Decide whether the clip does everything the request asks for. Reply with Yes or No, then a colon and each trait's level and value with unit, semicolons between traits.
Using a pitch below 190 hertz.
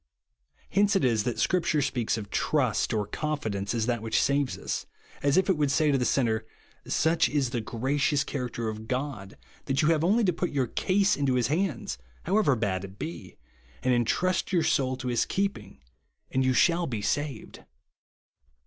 Yes: low, 135 Hz